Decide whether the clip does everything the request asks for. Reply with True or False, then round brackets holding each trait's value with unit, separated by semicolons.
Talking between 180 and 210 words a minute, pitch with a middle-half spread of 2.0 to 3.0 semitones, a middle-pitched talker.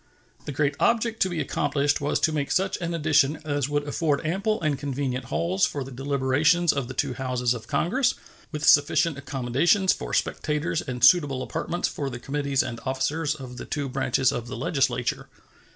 False (185 wpm; 3.4 semitones; 145 Hz)